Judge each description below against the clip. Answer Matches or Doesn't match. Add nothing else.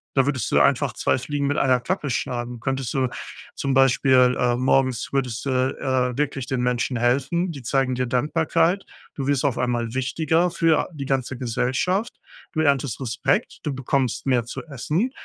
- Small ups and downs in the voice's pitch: Matches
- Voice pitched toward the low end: Matches